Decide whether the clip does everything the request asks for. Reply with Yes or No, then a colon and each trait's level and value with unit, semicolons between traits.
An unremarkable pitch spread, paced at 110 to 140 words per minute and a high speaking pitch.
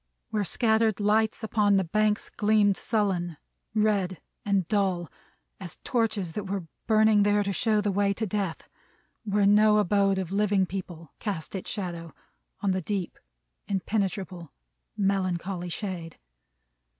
No: narrow, 2.2 semitones; slow, 135 wpm; high, 200 Hz